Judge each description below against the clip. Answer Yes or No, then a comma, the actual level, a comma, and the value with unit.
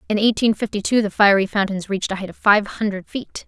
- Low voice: No, high, 205 Hz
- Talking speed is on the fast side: Yes, fast, 240 wpm